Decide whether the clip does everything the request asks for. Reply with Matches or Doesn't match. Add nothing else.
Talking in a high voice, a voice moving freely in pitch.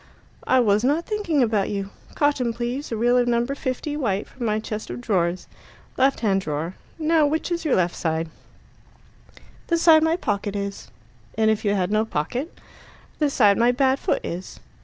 Matches